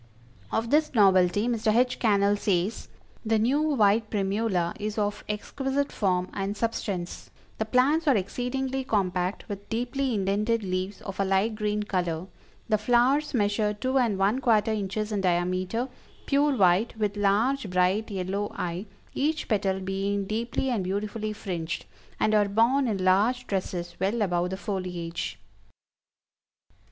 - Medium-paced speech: Yes, average, 145 wpm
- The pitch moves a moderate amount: Yes, average, 3.5 semitones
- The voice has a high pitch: Yes, high, 210 Hz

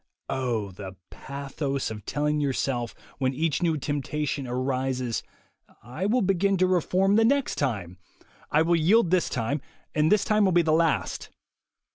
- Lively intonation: Yes, wide, 5.8 semitones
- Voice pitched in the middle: Yes, medium, 150 Hz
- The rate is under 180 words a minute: Yes, average, 150 wpm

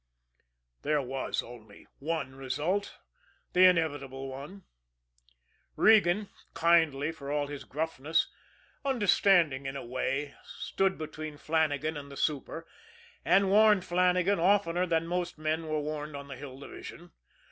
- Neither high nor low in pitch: Yes, medium, 155 Hz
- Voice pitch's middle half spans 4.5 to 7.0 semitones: No, average, 4.1 semitones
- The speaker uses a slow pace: Yes, slow, 125 wpm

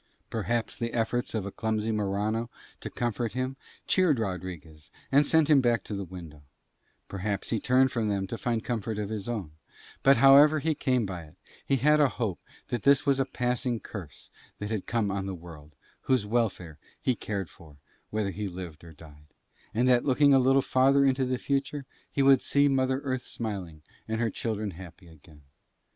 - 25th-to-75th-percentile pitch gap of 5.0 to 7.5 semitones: Yes, average, 5.3 semitones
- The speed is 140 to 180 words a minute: No, average, 190 wpm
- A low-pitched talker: Yes, low, 110 Hz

